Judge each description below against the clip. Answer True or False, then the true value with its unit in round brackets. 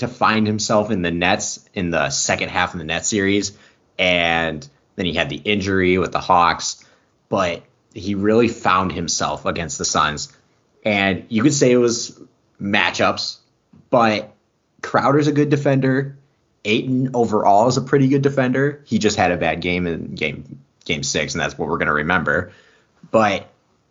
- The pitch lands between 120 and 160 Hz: False (105 Hz)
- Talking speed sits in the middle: True (170 wpm)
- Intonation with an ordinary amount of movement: False (6.0 semitones)